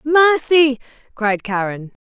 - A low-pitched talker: No, very high, 255 Hz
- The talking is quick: No, slow, 85 wpm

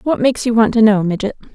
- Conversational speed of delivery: No, fast, 270 wpm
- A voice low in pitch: No, high, 225 Hz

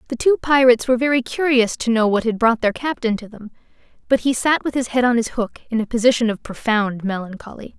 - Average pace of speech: No, fast, 230 wpm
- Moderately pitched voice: No, high, 235 Hz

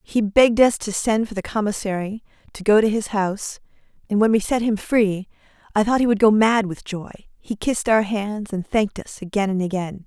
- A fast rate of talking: Yes, fast, 220 wpm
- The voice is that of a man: No, female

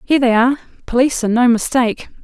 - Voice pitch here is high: Yes, high, 245 Hz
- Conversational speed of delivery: Yes, average, 160 wpm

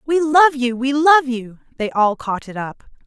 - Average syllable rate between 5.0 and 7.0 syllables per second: No, 4.3 syllables/s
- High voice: Yes, very high, 260 Hz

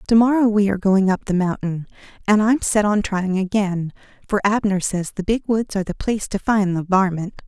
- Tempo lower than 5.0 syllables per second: No, 5.4 syllables/s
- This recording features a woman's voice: Yes, female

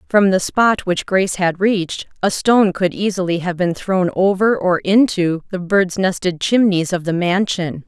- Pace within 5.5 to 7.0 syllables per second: No, 4.6 syllables/s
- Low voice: No, medium, 185 Hz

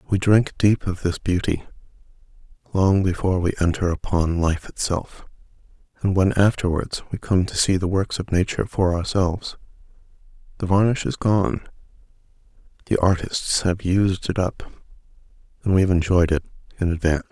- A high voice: No, very low, 95 Hz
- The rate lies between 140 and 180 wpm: Yes, average, 150 wpm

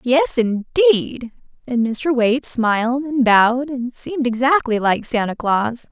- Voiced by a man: No, female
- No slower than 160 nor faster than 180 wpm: No, average, 140 wpm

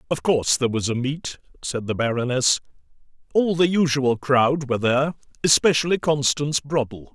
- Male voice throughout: Yes, male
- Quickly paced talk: No, average, 150 wpm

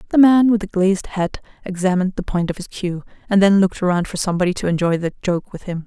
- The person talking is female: Yes, female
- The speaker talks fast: Yes, fast, 245 wpm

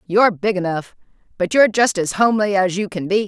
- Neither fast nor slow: No, fast, 220 wpm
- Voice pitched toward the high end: Yes, high, 195 Hz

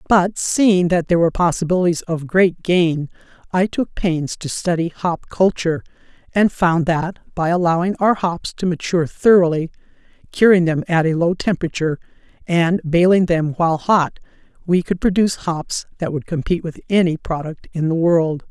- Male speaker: No, female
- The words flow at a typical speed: Yes, average, 160 wpm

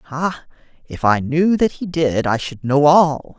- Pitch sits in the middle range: Yes, medium, 150 Hz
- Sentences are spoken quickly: No, average, 195 wpm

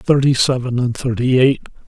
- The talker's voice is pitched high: No, low, 125 Hz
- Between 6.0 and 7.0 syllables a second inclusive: No, 4.9 syllables/s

